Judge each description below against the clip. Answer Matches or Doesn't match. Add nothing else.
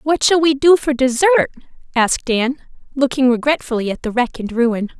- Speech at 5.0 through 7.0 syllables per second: Matches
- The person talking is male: Doesn't match